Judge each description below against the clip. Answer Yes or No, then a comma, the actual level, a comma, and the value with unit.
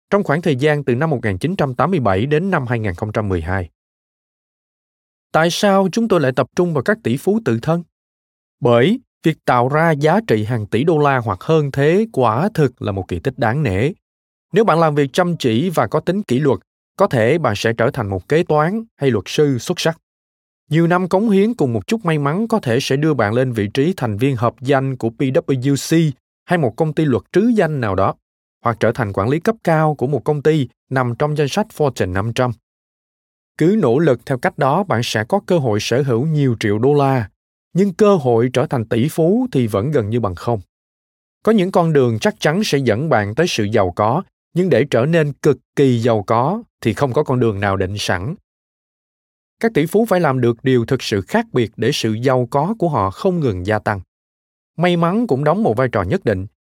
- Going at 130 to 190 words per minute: No, average, 220 wpm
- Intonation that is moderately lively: No, wide, 6.5 semitones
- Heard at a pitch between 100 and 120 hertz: No, low, 135 Hz